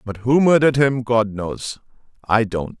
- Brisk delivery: No, average, 150 wpm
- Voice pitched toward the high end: No, low, 120 Hz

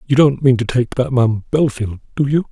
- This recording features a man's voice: Yes, male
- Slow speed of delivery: No, fast, 240 wpm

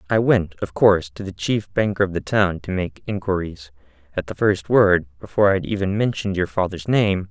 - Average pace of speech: No, fast, 215 wpm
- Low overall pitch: Yes, very low, 95 Hz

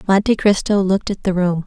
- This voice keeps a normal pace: No, fast, 215 wpm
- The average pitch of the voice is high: Yes, high, 195 Hz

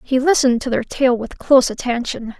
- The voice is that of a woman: Yes, female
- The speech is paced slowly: No, average, 200 wpm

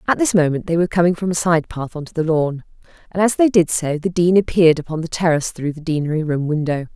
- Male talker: No, female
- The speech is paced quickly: Yes, fast, 260 wpm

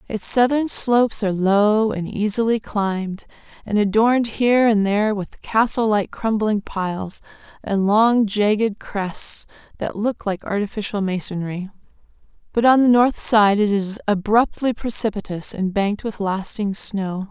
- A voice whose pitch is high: Yes, high, 210 Hz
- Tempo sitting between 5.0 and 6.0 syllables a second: No, 4.4 syllables/s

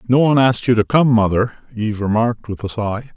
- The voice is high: No, low, 115 Hz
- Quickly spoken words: Yes, fast, 230 wpm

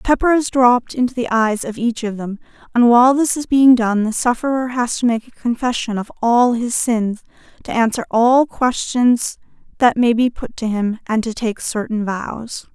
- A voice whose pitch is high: Yes, high, 240 Hz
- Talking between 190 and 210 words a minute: Yes, average, 200 wpm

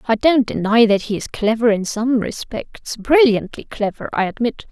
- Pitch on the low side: No, high, 230 Hz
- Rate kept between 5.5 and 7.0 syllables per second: No, 4.7 syllables/s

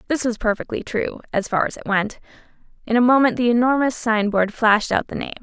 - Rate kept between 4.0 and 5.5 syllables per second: No, 6.0 syllables/s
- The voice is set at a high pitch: Yes, high, 230 Hz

